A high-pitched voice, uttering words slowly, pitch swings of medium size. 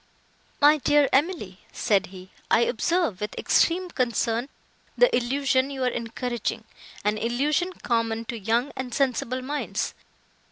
Yes: very high, 250 Hz; slow, 125 wpm; average, 4.1 semitones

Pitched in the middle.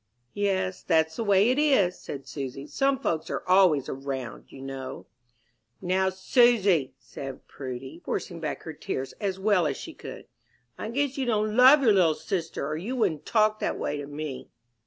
Yes: medium, 180 Hz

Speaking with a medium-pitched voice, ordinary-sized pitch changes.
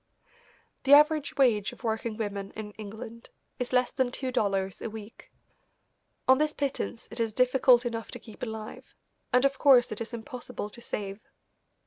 No: high, 235 Hz; average, 3.1 semitones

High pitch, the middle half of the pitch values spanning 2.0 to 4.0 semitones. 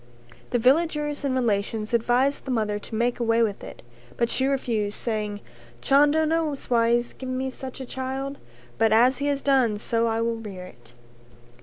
Yes: high, 240 Hz; average, 3.4 semitones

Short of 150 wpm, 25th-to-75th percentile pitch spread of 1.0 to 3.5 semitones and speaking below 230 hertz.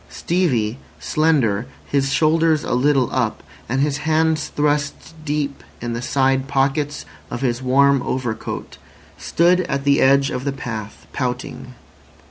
Yes: slow, 135 wpm; average, 2.8 semitones; medium, 140 Hz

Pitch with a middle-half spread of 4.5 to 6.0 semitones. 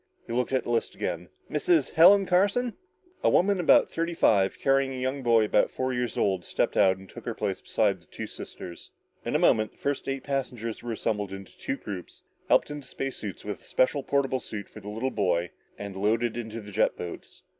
Yes: average, 5.0 semitones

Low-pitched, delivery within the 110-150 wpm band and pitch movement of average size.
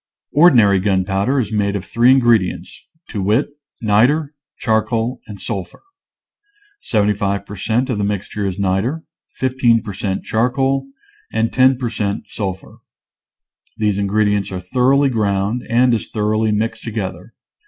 Yes: low, 110 Hz; average, 145 wpm; average, 3.5 semitones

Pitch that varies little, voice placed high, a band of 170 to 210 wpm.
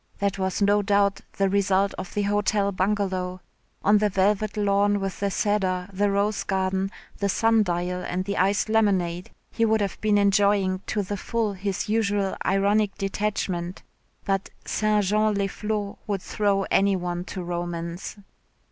No: narrow, 1.6 semitones; high, 200 Hz; average, 160 wpm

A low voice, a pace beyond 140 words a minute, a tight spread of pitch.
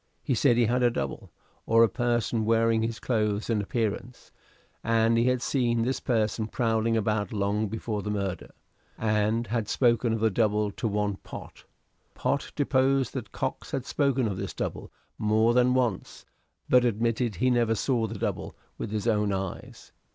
Yes: low, 115 Hz; average, 175 wpm; narrow, 2.3 semitones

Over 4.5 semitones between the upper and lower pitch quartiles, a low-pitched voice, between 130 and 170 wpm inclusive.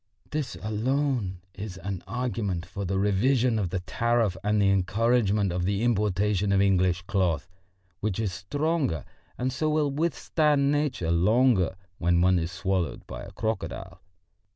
Yes: average, 5.1 semitones; low, 100 Hz; average, 150 wpm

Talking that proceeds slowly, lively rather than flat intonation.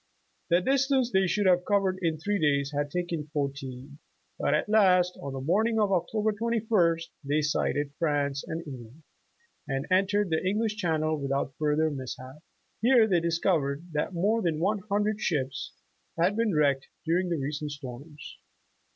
No: average, 170 wpm; wide, 5.7 semitones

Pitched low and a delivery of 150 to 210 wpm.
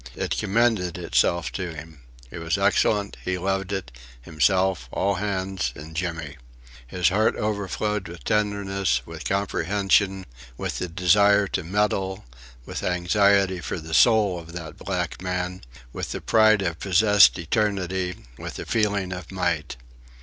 No: very low, 95 Hz; average, 140 wpm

